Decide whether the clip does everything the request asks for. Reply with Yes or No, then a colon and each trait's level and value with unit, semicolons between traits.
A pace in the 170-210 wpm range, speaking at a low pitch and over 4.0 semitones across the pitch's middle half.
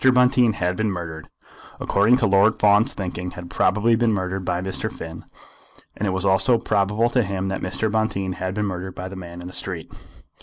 No: average, 200 wpm; very low, 95 Hz; average, 3.1 semitones